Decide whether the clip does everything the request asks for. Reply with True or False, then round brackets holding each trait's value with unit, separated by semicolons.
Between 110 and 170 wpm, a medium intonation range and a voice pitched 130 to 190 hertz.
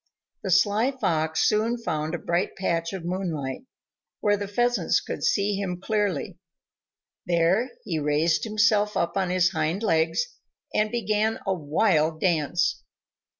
True (140 wpm; 4.3 semitones; 185 Hz)